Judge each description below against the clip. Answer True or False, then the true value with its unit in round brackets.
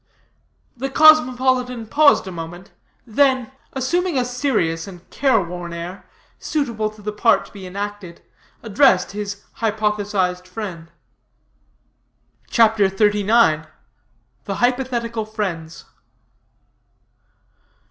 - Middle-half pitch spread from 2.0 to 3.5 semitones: False (5.0 semitones)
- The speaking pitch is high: True (215 Hz)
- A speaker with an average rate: False (95 wpm)